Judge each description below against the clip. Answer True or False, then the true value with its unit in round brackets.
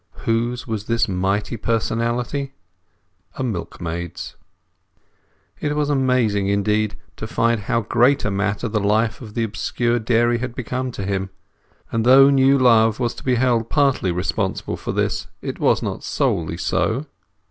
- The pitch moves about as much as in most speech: True (3.3 semitones)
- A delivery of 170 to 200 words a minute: False (150 wpm)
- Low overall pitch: True (115 Hz)